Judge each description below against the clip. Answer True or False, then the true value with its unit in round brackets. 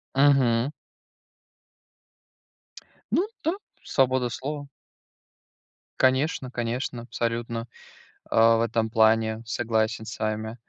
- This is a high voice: False (115 Hz)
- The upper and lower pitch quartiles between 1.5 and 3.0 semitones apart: True (2.5 semitones)